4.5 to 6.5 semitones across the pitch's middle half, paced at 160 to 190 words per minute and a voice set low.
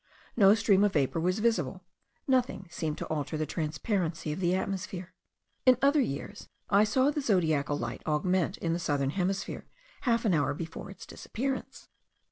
No: average, 5.3 semitones; average, 165 wpm; medium, 185 Hz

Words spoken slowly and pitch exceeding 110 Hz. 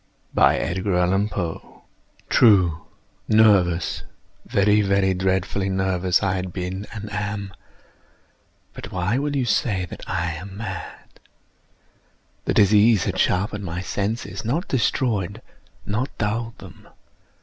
No: slow, 95 wpm; low, 100 Hz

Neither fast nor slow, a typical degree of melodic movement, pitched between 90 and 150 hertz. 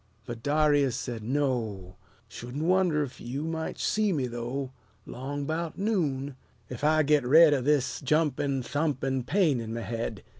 Yes: average, 155 wpm; average, 3.8 semitones; medium, 140 Hz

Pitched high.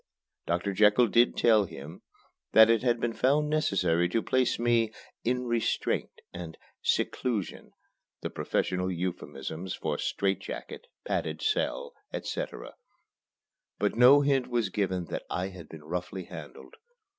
No: low, 105 Hz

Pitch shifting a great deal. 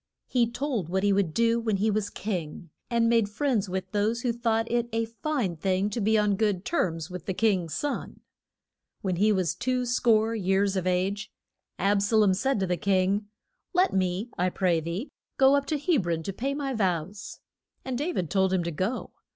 No: average, 4.0 semitones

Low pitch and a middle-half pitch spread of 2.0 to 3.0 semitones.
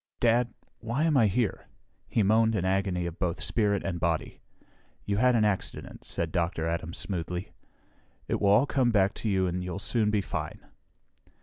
No: low, 100 Hz; average, 4.1 semitones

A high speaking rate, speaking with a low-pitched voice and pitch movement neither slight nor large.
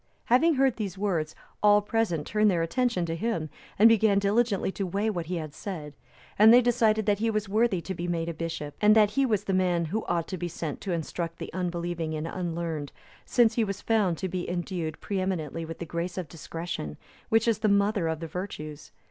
No: fast, 215 wpm; medium, 185 Hz; average, 4.2 semitones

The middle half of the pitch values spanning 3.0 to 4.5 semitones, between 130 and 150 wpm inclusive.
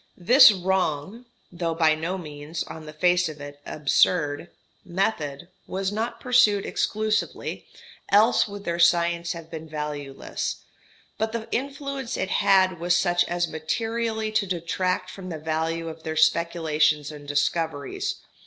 Yes: average, 4.0 semitones; average, 140 wpm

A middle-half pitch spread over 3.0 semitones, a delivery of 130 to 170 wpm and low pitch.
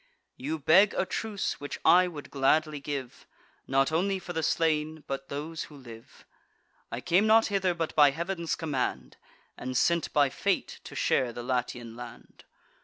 No: average, 4.2 semitones; average, 165 wpm; medium, 155 Hz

